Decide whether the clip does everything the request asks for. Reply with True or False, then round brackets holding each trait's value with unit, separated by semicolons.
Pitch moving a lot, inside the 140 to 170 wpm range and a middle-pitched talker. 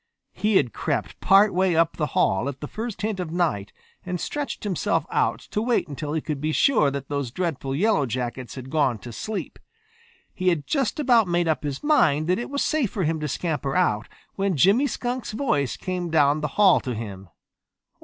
False (6.6 semitones; 205 wpm; 165 Hz)